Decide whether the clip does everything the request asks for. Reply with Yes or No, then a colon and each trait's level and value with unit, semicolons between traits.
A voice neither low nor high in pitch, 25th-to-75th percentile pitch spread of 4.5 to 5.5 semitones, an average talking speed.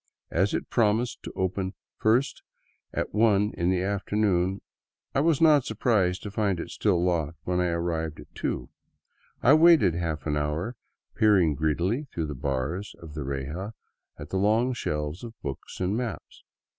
No: very low, 95 Hz; average, 5.1 semitones; average, 165 wpm